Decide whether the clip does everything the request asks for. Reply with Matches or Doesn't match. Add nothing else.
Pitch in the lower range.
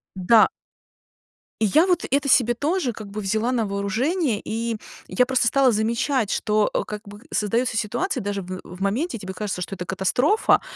Doesn't match